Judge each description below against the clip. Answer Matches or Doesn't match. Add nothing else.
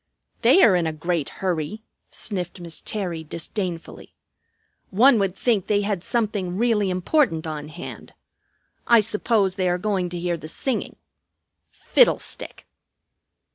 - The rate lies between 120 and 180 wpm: Matches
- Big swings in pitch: Doesn't match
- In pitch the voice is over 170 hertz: Matches